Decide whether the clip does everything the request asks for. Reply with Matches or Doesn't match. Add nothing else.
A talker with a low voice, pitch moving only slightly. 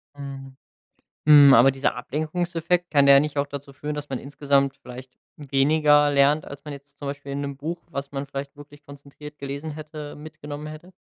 Doesn't match